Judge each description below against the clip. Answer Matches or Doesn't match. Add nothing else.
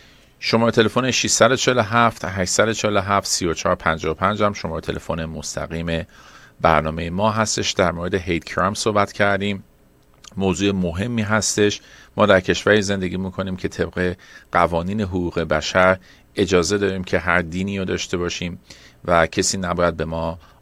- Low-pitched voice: Matches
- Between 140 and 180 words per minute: Doesn't match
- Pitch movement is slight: Doesn't match